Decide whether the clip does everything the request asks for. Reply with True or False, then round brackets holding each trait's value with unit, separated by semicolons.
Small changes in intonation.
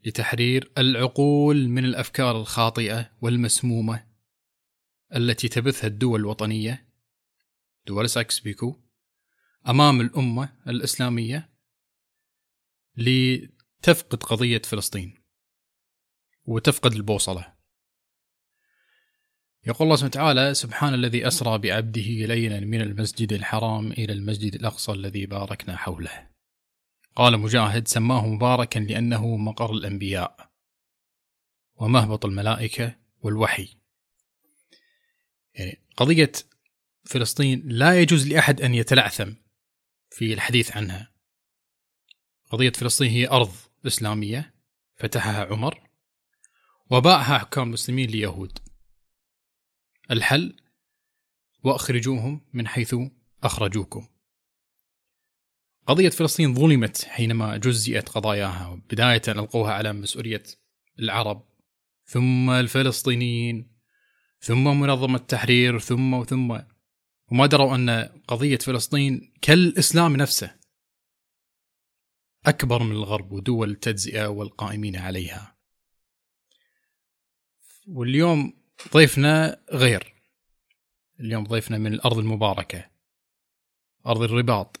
False (3.4 semitones)